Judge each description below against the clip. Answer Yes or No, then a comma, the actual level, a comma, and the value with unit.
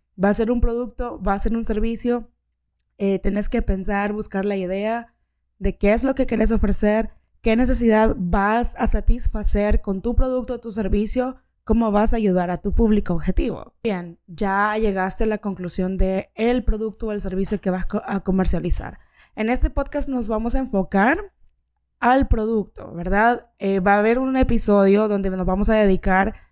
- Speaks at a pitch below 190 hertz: No, high, 210 Hz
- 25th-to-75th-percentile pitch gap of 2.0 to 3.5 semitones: Yes, average, 2.9 semitones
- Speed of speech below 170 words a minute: No, average, 180 wpm